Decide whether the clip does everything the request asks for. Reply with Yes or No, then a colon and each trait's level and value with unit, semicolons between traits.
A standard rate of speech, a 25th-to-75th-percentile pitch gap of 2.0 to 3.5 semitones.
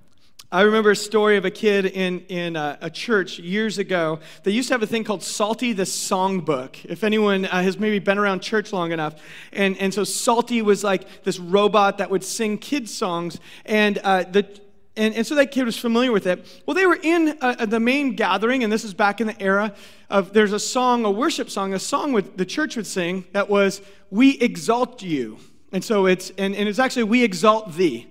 No: fast, 220 wpm; average, 3.0 semitones